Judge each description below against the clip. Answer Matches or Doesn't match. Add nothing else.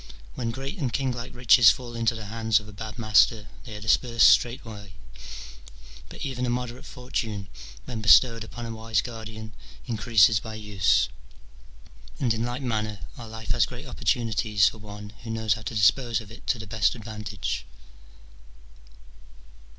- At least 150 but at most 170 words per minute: Matches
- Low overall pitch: Matches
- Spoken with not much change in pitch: Matches